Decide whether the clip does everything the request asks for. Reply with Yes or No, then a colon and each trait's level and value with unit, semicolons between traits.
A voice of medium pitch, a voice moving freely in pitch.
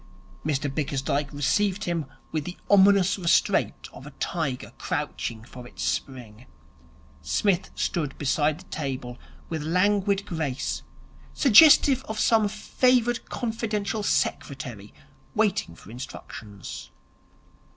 Yes: medium, 170 Hz; wide, 7.4 semitones